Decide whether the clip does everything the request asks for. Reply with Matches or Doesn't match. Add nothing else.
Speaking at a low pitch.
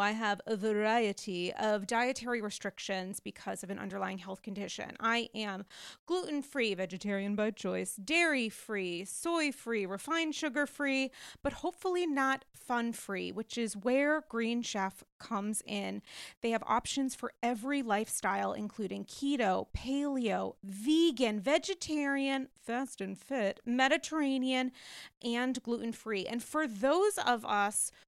Doesn't match